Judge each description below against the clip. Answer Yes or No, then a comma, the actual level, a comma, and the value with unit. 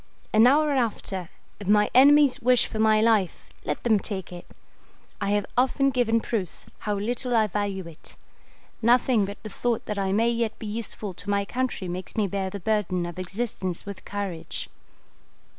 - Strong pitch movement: No, average, 3.4 semitones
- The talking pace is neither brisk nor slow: Yes, average, 175 wpm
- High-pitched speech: Yes, high, 210 Hz